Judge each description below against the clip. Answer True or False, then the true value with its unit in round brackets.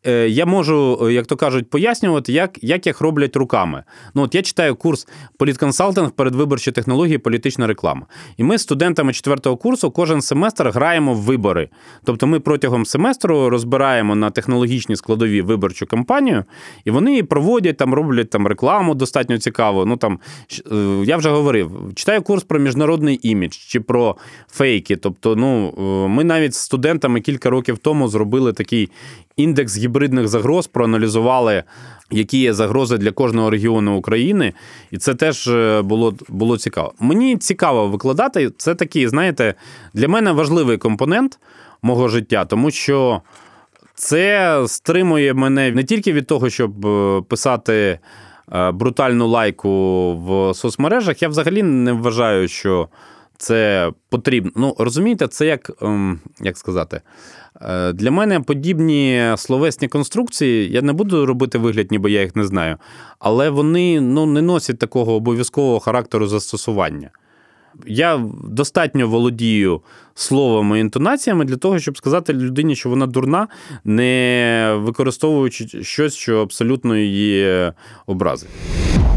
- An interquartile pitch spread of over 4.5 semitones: True (5.0 semitones)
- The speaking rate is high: False (135 wpm)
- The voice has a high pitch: False (125 Hz)